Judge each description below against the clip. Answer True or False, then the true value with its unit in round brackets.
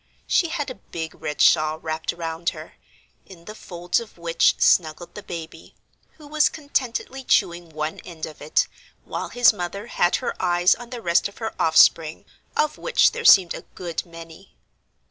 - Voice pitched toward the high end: False (175 Hz)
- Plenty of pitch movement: True (6.1 semitones)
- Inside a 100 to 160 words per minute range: False (175 wpm)